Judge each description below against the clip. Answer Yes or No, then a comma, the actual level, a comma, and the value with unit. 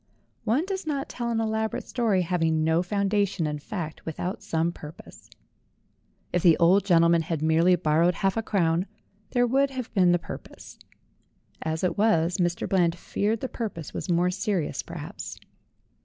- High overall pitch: No, medium, 180 Hz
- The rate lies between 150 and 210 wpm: Yes, average, 160 wpm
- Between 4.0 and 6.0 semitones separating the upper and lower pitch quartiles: Yes, average, 4.7 semitones